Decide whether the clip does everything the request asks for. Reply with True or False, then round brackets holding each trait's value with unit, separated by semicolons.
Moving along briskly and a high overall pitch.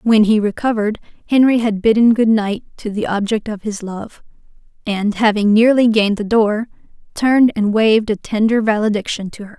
False (175 wpm; 215 Hz)